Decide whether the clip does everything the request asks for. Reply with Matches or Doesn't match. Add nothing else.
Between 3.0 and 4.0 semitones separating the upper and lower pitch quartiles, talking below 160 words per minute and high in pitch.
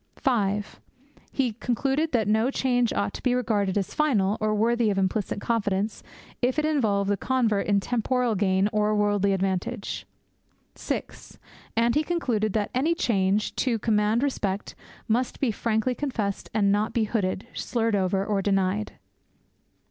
Matches